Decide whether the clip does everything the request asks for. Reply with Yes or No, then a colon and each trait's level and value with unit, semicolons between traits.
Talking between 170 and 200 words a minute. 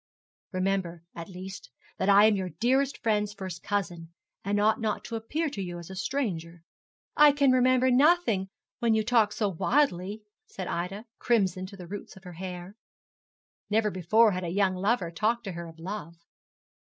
Yes: average, 180 wpm